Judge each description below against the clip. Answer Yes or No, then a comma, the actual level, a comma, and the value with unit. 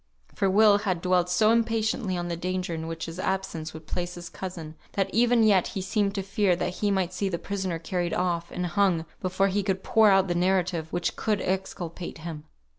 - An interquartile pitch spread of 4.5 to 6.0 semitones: No, narrow, 2.4 semitones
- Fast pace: Yes, fast, 210 wpm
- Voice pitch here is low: No, medium, 185 Hz